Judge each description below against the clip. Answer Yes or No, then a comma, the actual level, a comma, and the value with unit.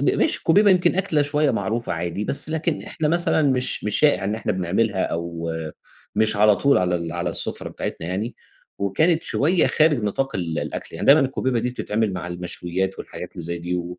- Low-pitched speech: Yes, low, 105 Hz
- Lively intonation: Yes, wide, 8.5 semitones